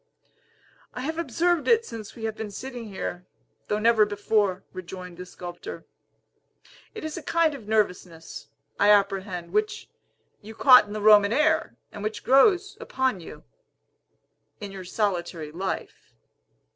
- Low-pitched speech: No, high, 210 Hz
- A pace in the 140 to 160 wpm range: Yes, average, 145 wpm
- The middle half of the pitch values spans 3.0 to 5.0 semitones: No, wide, 5.6 semitones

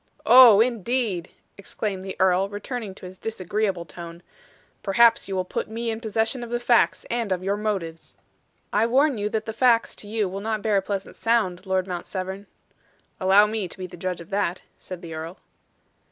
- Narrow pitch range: No, average, 3.3 semitones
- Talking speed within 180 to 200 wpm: Yes, average, 195 wpm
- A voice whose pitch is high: Yes, high, 200 Hz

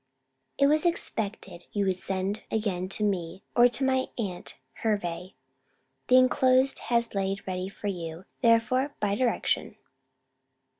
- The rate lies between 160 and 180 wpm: No, slow, 135 wpm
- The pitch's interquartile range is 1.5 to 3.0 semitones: No, average, 5.1 semitones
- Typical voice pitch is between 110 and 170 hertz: No, high, 210 Hz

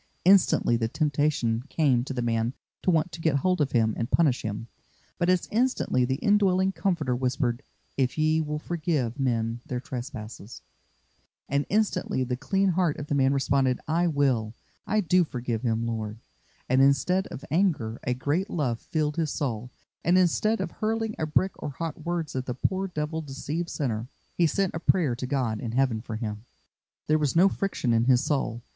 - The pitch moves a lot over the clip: Yes, wide, 5.7 semitones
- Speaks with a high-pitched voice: No, medium, 140 Hz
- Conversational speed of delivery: Yes, average, 185 wpm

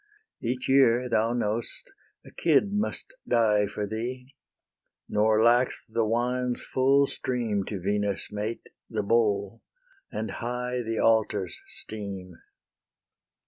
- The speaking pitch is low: Yes, low, 115 Hz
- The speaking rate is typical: No, slow, 115 wpm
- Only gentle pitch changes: No, average, 3.0 semitones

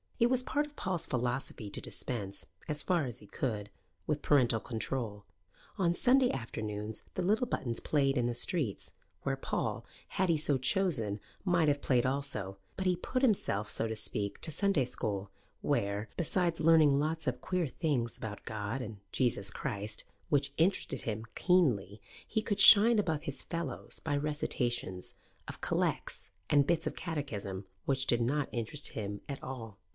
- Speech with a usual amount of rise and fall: No, wide, 7.1 semitones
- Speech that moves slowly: No, average, 165 wpm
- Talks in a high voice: No, low, 135 Hz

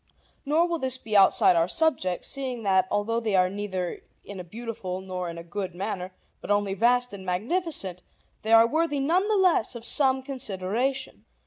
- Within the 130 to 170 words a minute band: No, average, 185 wpm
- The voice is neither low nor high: No, high, 220 Hz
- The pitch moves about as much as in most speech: No, wide, 6.1 semitones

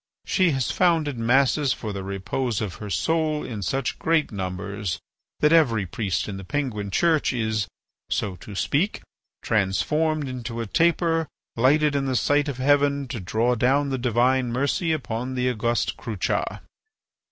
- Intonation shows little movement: No, average, 5.3 semitones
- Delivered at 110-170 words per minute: Yes, average, 155 wpm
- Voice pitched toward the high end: No, low, 130 Hz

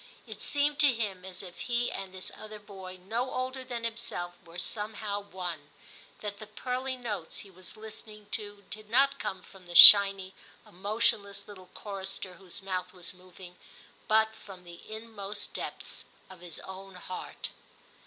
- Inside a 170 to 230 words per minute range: No, average, 160 wpm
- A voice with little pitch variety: No, average, 3.0 semitones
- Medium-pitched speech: No, high, 200 Hz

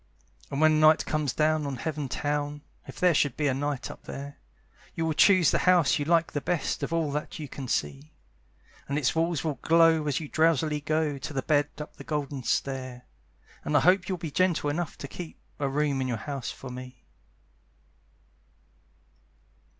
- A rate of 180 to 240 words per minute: Yes, average, 190 wpm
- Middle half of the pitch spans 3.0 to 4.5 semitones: No, narrow, 2.6 semitones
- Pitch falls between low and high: Yes, medium, 150 Hz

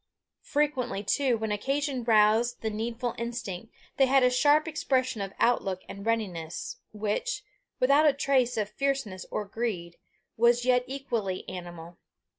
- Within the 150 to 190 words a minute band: No, average, 140 wpm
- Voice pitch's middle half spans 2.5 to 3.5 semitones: No, average, 4.5 semitones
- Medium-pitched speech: No, high, 235 Hz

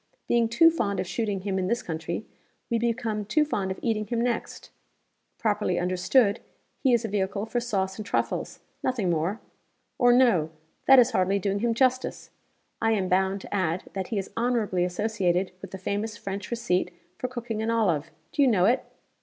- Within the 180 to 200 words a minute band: Yes, average, 185 wpm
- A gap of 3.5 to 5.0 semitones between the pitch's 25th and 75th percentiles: Yes, average, 3.8 semitones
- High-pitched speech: Yes, high, 210 Hz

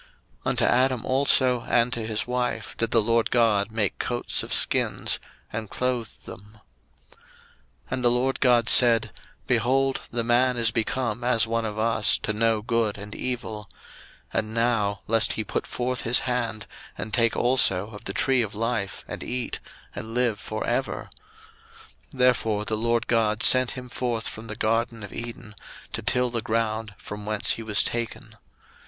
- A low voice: Yes, low, 115 Hz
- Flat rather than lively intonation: Yes, narrow, 2.1 semitones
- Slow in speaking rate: No, average, 170 wpm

